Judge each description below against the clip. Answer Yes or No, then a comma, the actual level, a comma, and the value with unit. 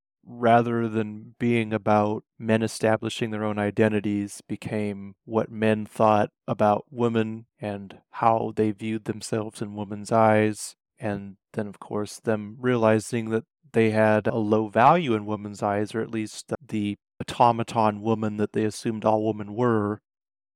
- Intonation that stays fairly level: Yes, narrow, 1.3 semitones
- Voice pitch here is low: Yes, low, 110 Hz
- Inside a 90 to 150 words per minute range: Yes, average, 145 wpm